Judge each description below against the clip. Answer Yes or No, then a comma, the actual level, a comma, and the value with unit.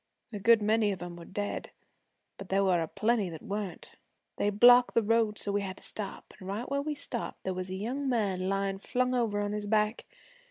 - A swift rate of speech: Yes, fast, 225 wpm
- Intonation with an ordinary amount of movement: Yes, average, 3.0 semitones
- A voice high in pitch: Yes, high, 205 Hz